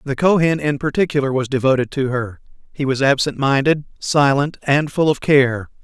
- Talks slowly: No, average, 175 wpm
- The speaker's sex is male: Yes, male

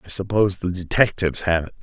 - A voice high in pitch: No, very low, 90 Hz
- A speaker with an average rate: Yes, average, 195 wpm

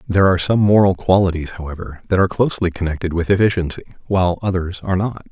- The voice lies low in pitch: Yes, very low, 90 Hz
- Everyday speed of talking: Yes, average, 180 wpm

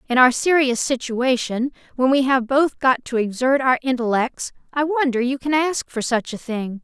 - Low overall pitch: No, very high, 255 Hz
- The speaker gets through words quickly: No, average, 195 wpm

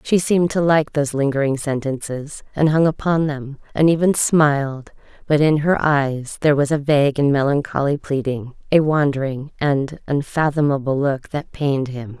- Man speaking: No, female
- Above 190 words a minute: No, average, 150 wpm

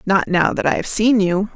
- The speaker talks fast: Yes, fast, 270 wpm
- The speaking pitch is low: No, high, 195 Hz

